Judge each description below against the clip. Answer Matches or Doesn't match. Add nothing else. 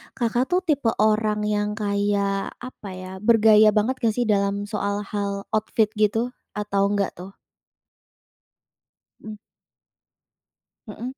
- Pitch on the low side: Doesn't match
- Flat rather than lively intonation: Matches